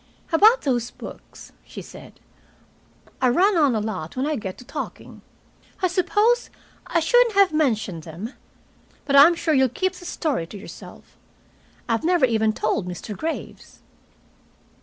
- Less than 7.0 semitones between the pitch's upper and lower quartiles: No, wide, 8.4 semitones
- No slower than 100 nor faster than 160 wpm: Yes, average, 150 wpm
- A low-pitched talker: No, very high, 275 Hz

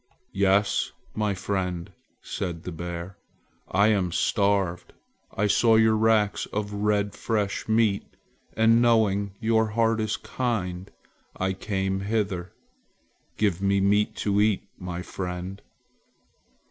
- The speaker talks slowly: Yes, slow, 120 wpm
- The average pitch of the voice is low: Yes, low, 100 Hz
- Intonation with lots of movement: No, narrow, 2.4 semitones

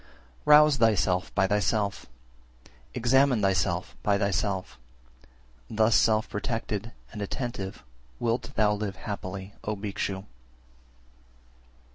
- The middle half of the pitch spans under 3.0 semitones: Yes, narrow, 2.6 semitones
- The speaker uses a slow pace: Yes, slow, 100 wpm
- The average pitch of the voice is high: No, low, 105 Hz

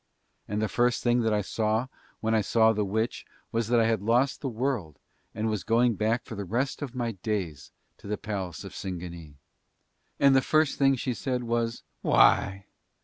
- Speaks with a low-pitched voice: Yes, low, 110 Hz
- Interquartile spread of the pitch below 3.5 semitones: Yes, average, 3.1 semitones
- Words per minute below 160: No, average, 200 wpm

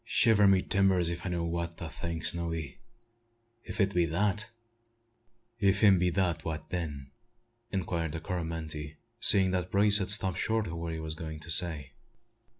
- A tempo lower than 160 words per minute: No, average, 175 wpm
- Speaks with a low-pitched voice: Yes, very low, 85 Hz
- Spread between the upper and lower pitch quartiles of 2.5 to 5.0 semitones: Yes, average, 3.2 semitones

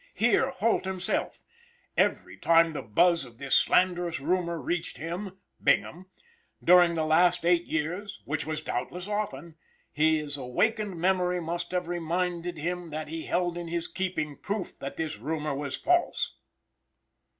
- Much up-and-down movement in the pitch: No, narrow, 2.5 semitones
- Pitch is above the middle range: No, medium, 170 Hz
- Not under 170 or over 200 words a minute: No, average, 145 wpm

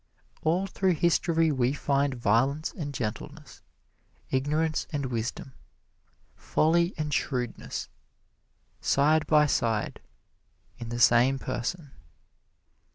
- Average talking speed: No, slow, 95 wpm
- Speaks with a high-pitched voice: No, medium, 145 Hz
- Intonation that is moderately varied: Yes, average, 4.3 semitones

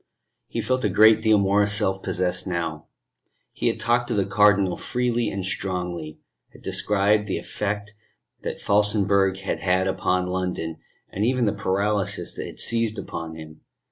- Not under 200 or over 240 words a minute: No, average, 160 wpm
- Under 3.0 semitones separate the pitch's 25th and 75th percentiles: Yes, narrow, 2.4 semitones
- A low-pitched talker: Yes, low, 100 Hz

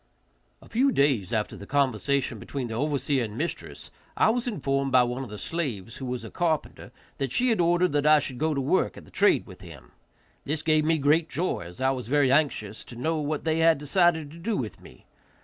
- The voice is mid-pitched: Yes, medium, 145 Hz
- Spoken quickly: Yes, fast, 225 wpm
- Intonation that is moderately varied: Yes, average, 4.6 semitones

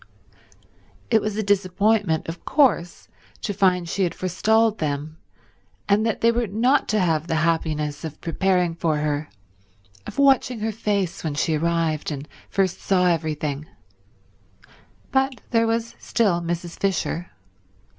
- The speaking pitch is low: No, medium, 180 Hz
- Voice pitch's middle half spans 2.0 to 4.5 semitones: No, average, 5.1 semitones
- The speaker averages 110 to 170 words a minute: Yes, average, 140 wpm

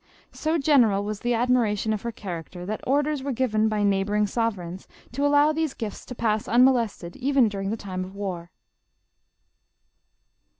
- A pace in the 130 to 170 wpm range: Yes, average, 165 wpm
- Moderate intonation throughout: Yes, average, 4.5 semitones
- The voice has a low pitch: No, high, 220 Hz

